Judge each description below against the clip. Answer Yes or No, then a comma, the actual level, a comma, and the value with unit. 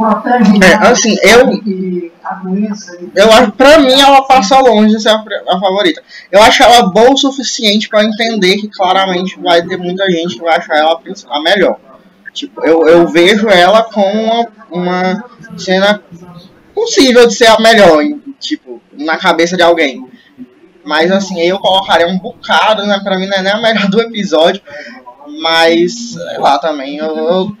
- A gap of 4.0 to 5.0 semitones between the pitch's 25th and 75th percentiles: Yes, average, 4.5 semitones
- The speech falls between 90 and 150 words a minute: No, average, 165 wpm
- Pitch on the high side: Yes, high, 195 Hz